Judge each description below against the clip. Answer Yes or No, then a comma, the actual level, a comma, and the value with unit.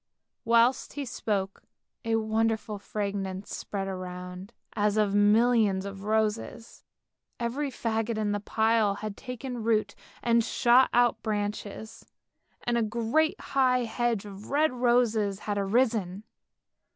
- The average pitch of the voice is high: Yes, high, 220 Hz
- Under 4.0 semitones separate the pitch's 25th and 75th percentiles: Yes, average, 2.7 semitones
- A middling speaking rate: No, slow, 125 wpm